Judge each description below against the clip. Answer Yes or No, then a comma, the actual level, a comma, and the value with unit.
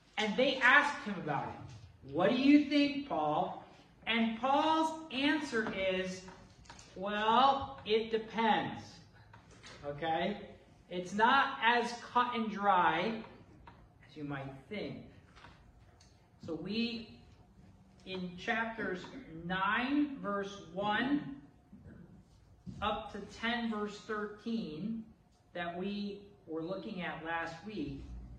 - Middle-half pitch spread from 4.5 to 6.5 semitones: Yes, average, 5.0 semitones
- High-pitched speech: Yes, high, 210 Hz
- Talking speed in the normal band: No, slow, 100 wpm